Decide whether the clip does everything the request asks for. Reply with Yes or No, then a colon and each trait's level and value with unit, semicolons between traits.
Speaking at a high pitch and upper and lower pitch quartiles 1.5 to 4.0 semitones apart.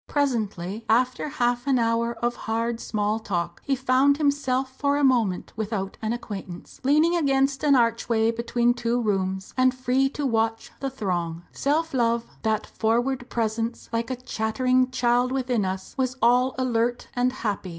Yes: high, 240 Hz; average, 2.8 semitones